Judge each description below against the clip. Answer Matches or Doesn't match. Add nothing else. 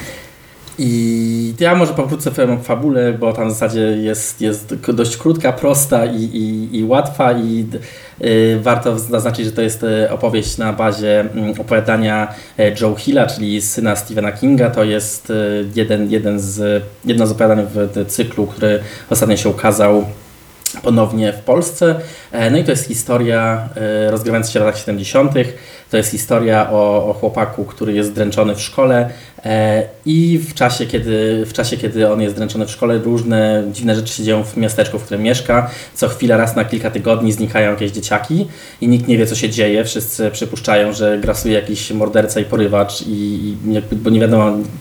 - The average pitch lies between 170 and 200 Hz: Doesn't match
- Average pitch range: Doesn't match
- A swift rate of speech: Matches